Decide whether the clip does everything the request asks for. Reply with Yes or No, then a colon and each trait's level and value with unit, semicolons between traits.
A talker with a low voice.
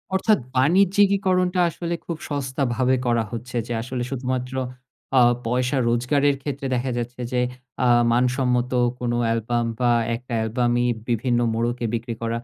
Yes: low, 125 Hz